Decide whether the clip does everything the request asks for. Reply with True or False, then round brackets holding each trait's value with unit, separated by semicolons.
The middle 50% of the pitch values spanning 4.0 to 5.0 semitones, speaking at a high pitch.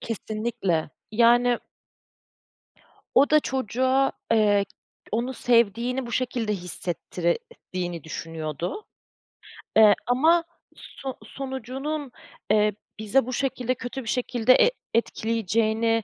False (3.4 semitones; 235 Hz)